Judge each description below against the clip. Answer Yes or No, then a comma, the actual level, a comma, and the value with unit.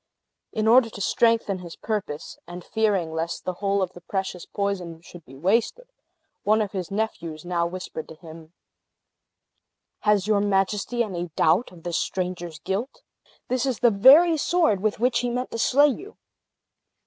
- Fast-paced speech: No, average, 165 wpm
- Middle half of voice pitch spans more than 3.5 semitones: Yes, average, 4.7 semitones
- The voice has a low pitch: No, high, 200 Hz